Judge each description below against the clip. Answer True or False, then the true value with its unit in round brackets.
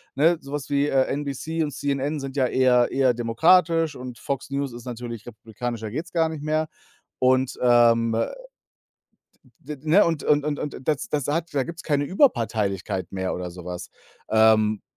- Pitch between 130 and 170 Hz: True (135 Hz)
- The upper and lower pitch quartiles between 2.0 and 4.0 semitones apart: False (4.6 semitones)